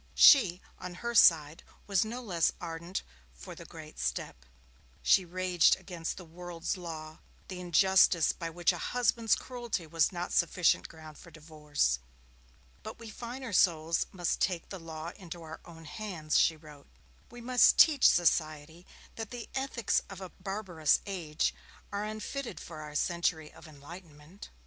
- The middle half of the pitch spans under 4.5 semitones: Yes, average, 3.9 semitones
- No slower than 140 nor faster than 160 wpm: Yes, average, 155 wpm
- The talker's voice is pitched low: No, medium, 175 Hz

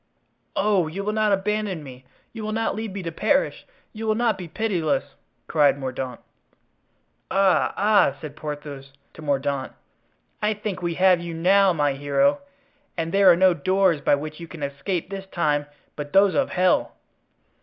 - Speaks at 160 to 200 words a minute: Yes, average, 170 wpm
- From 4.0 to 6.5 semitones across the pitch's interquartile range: Yes, wide, 5.4 semitones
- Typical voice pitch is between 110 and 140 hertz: No, medium, 180 Hz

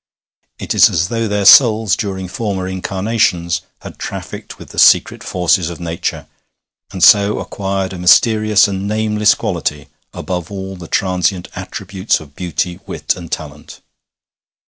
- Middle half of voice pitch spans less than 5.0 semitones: Yes, average, 2.8 semitones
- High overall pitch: No, very low, 95 Hz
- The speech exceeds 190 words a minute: No, average, 140 wpm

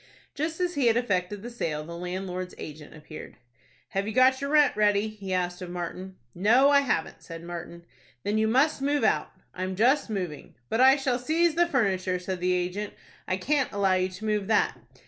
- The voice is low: No, high, 205 Hz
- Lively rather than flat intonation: Yes, wide, 6.1 semitones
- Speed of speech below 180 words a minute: No, average, 200 wpm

